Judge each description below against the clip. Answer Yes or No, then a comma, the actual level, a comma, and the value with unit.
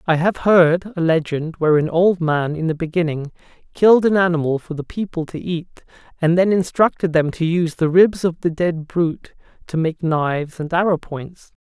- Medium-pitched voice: Yes, medium, 170 Hz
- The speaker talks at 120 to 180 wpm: No, average, 190 wpm